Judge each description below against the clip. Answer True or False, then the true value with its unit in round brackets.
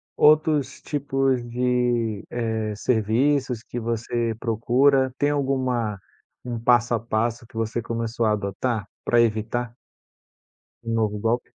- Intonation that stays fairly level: True (2.3 semitones)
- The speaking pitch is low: True (120 Hz)